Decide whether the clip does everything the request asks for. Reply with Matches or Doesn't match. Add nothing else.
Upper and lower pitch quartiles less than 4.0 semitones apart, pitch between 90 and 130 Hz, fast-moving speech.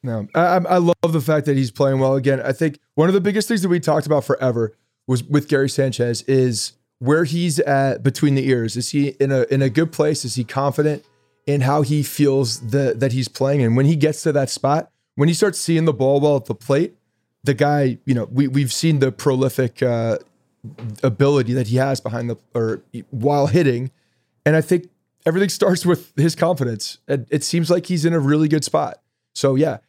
Doesn't match